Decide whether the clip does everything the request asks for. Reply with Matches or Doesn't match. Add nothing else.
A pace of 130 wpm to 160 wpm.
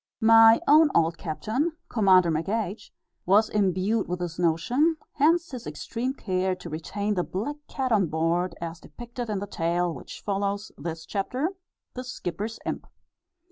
Matches